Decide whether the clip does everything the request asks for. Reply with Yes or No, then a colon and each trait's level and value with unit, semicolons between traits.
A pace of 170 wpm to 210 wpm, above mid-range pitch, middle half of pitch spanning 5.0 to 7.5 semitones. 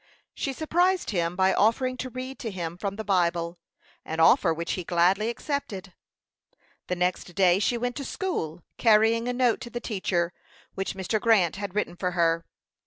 Yes: average, 175 wpm; high, 195 Hz; average, 5.3 semitones